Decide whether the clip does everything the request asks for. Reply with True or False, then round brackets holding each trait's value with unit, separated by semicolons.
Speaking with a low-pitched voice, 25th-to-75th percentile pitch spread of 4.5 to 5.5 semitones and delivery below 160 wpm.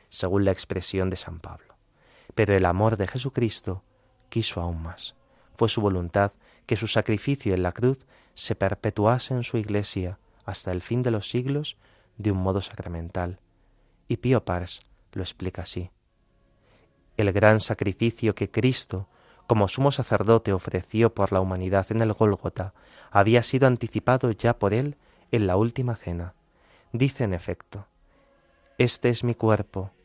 False (105 Hz; 3.9 semitones; 150 wpm)